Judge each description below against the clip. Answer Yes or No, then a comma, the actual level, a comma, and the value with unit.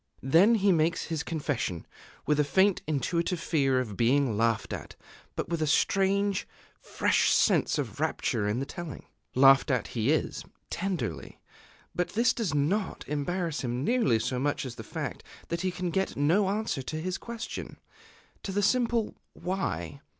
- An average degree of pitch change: No, wide, 6.3 semitones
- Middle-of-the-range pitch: Yes, medium, 160 Hz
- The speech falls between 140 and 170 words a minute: Yes, average, 165 wpm